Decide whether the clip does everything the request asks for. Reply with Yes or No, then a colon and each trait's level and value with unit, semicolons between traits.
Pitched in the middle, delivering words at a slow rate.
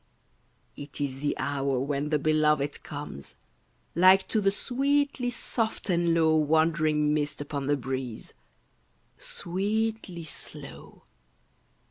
Yes: medium, 155 Hz; slow, 110 wpm